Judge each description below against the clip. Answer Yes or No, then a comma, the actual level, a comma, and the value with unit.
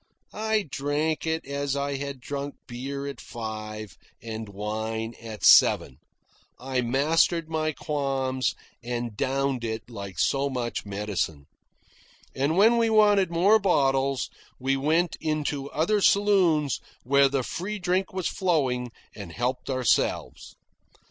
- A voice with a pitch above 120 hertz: Yes, medium, 140 Hz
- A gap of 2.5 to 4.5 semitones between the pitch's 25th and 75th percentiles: No, average, 5.1 semitones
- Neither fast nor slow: No, slow, 130 wpm